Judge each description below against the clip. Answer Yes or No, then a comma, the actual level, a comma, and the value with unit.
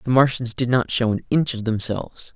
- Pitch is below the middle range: Yes, low, 120 Hz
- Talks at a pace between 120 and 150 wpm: No, fast, 230 wpm